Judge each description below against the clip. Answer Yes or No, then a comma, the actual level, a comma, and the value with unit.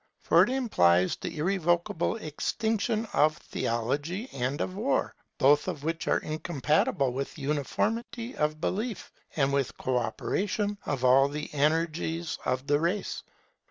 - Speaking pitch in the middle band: Yes, medium, 155 Hz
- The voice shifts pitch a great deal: Yes, wide, 6.3 semitones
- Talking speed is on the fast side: No, slow, 135 wpm